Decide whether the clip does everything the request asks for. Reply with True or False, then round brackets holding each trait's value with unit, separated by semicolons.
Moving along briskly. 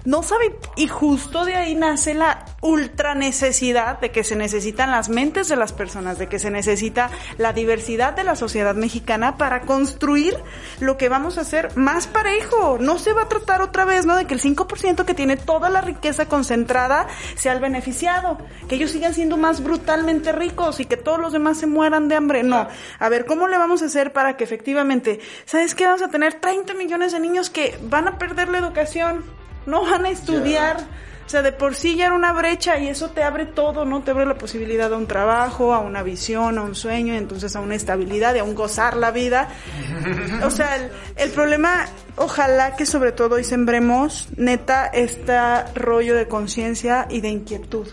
True (205 wpm)